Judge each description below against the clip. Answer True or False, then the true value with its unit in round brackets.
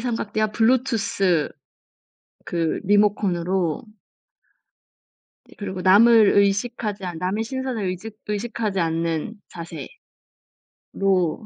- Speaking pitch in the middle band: False (200 Hz)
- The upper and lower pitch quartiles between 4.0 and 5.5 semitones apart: False (3.5 semitones)